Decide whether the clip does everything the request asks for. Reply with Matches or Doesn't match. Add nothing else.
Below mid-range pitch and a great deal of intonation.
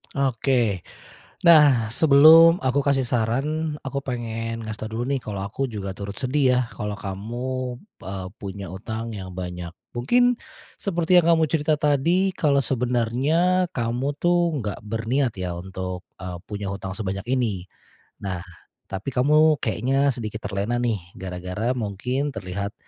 Matches